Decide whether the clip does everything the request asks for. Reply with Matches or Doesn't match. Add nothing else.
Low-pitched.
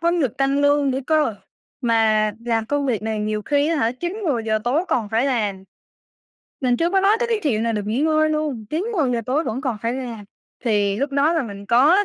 Doesn't match